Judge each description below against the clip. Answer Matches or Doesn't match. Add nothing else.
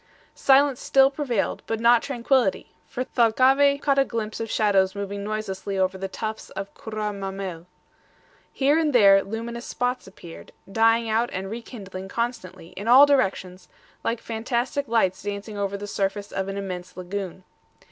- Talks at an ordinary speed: Matches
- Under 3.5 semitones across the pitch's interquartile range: Doesn't match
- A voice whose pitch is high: Matches